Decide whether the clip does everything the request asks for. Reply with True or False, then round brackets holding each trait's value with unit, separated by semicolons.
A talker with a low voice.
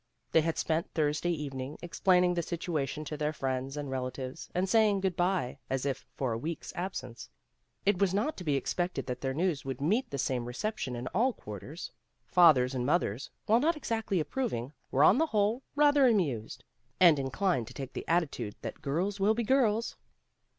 False (160 Hz)